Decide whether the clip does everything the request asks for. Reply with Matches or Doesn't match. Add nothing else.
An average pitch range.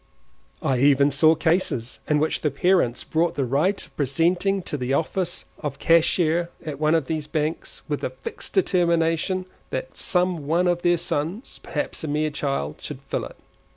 Matches